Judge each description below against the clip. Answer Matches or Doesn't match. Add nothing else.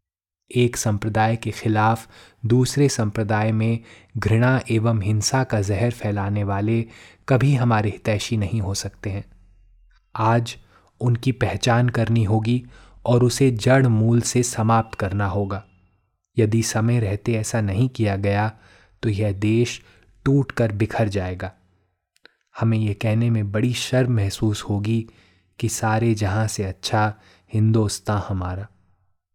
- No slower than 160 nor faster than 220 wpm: Doesn't match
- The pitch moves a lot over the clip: Doesn't match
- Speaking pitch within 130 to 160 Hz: Doesn't match